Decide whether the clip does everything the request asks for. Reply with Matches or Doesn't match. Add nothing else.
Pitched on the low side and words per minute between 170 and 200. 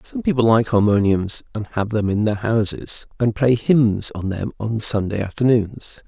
Matches